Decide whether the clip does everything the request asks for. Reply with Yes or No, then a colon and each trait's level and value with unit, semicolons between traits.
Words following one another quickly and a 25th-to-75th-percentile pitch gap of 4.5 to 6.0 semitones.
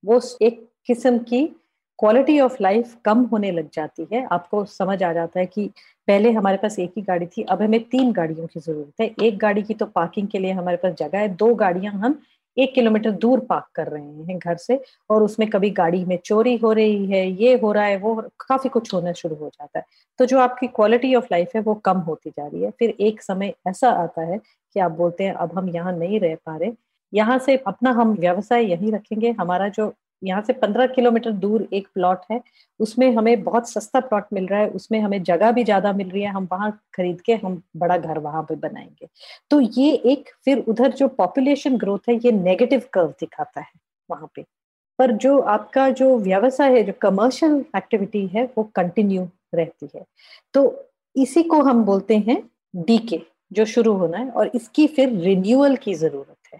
Yes: fast, 210 wpm; average, 4.8 semitones